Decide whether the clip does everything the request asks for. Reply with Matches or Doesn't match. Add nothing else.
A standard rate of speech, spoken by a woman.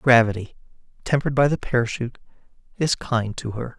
Doesn't match